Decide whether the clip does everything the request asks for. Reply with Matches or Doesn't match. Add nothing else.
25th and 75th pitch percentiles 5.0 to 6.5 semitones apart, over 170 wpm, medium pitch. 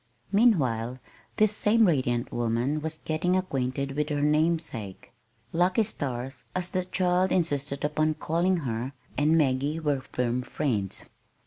Doesn't match